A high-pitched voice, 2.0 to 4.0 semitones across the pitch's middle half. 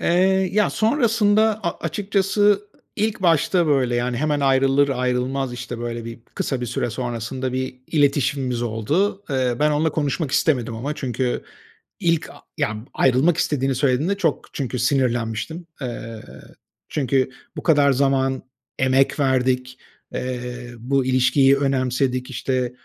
No: low, 135 Hz; average, 3.7 semitones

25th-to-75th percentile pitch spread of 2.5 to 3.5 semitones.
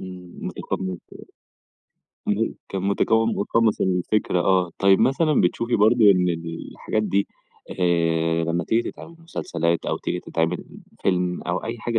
No: average, 4.4 semitones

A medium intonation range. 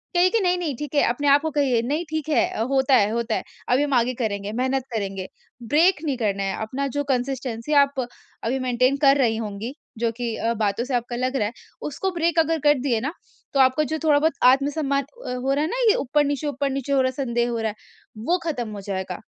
Yes: average, 3.7 semitones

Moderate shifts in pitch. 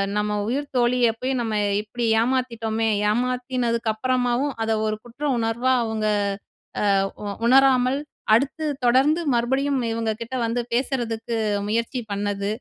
No: narrow, 2.3 semitones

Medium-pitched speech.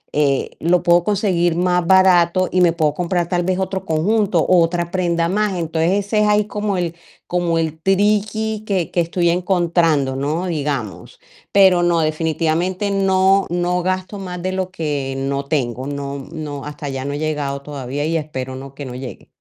Yes: medium, 170 Hz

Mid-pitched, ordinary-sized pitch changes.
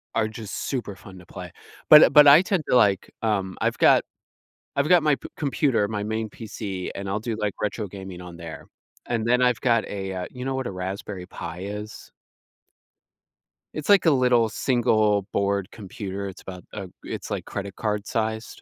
No: low, 105 Hz; average, 4.1 semitones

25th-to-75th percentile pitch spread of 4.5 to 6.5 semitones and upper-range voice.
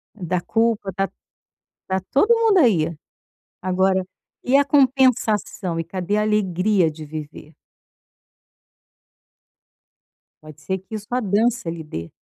Yes: wide, 5.4 semitones; high, 195 Hz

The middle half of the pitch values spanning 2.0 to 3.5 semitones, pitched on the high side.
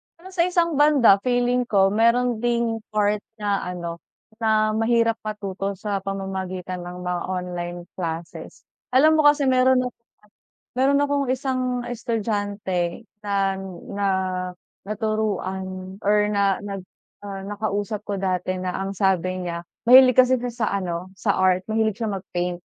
No: average, 4.4 semitones; high, 205 Hz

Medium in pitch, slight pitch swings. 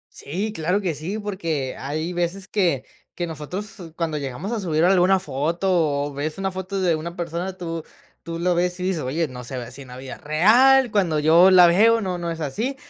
No: medium, 170 Hz; average, 3.7 semitones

